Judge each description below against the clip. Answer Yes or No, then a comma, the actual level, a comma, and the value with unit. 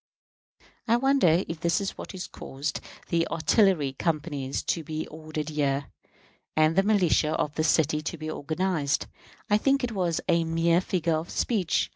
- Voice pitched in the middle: Yes, medium, 165 Hz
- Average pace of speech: Yes, average, 160 wpm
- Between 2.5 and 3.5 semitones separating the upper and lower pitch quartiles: Yes, average, 3.1 semitones